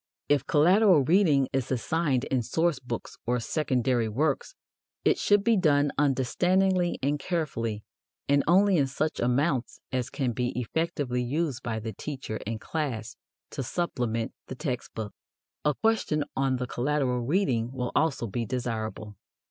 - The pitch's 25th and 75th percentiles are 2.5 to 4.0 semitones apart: No, average, 4.6 semitones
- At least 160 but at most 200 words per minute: No, average, 150 wpm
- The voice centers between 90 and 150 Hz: Yes, low, 135 Hz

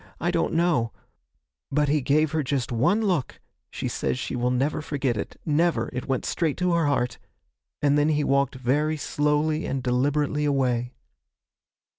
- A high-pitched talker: No, medium, 145 Hz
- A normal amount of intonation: Yes, average, 3.3 semitones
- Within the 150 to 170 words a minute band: Yes, average, 165 wpm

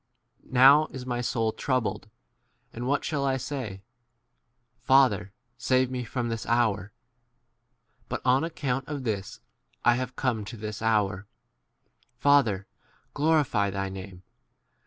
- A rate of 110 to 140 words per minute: Yes, slow, 135 wpm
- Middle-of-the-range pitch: No, low, 120 Hz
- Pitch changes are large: No, average, 4.0 semitones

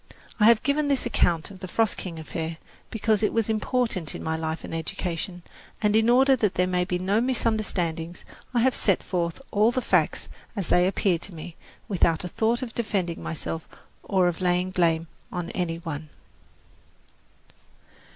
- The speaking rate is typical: Yes, average, 175 wpm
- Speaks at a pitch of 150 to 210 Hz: Yes, medium, 185 Hz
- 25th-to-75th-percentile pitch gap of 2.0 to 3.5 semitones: No, average, 4.9 semitones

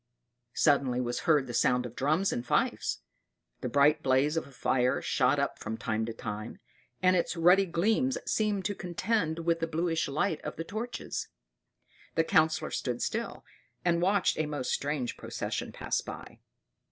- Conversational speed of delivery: Yes, average, 165 wpm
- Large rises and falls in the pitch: Yes, wide, 5.7 semitones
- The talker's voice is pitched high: No, medium, 155 Hz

